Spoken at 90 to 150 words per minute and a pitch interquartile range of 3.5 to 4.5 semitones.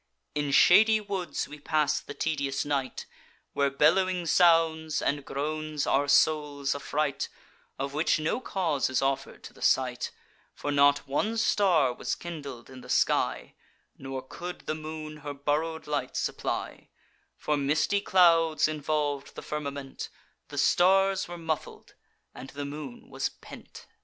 No: average, 140 wpm; average, 2.7 semitones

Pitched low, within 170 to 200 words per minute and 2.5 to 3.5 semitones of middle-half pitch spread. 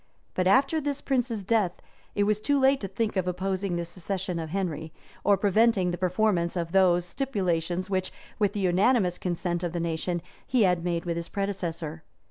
No: medium, 185 Hz; average, 185 wpm; average, 3.1 semitones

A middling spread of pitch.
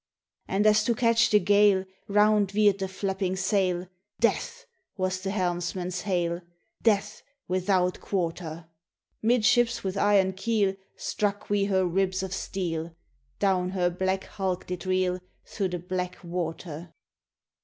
No: narrow, 2.2 semitones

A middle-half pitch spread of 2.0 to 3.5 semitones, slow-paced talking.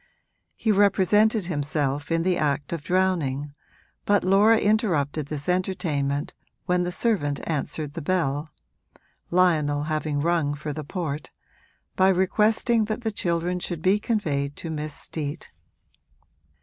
No: average, 4.5 semitones; slow, 130 wpm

